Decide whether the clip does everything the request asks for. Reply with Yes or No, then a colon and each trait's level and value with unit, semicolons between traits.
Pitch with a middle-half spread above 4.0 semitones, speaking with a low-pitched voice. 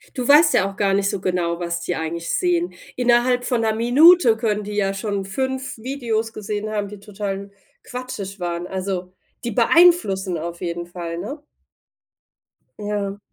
No: average, 4.6 semitones; high, 205 Hz